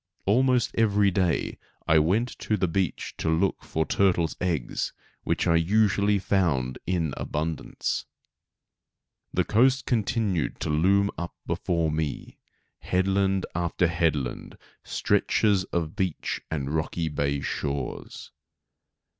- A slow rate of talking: Yes, slow, 120 wpm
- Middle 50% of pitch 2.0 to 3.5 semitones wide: No, average, 4.0 semitones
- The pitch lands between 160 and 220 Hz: No, very low, 90 Hz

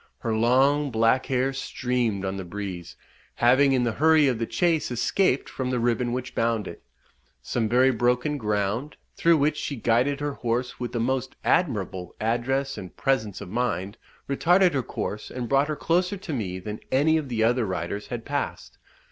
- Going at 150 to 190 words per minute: Yes, average, 180 wpm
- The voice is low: Yes, low, 125 Hz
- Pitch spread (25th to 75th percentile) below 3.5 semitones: No, average, 4.0 semitones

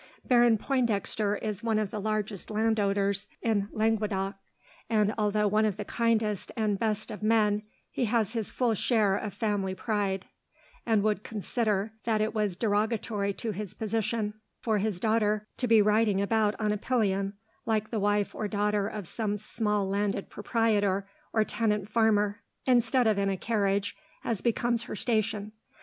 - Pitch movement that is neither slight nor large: No, narrow, 1.6 semitones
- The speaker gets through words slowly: No, average, 165 wpm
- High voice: Yes, high, 210 Hz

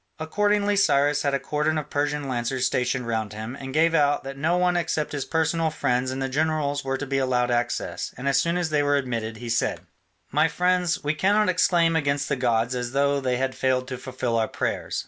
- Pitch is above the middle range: No, medium, 140 Hz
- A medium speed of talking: No, fast, 220 wpm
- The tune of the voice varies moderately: Yes, average, 3.8 semitones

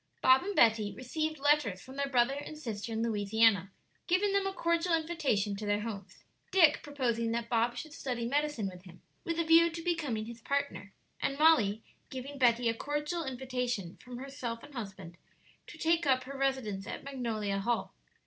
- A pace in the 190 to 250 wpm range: No, average, 180 wpm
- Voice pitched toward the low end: No, very high, 255 Hz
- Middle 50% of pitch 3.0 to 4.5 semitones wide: No, average, 5.1 semitones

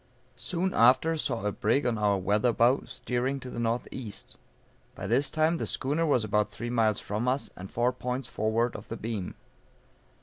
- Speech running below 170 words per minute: No, average, 180 wpm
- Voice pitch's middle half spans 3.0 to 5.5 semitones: Yes, average, 3.4 semitones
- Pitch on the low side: Yes, low, 120 Hz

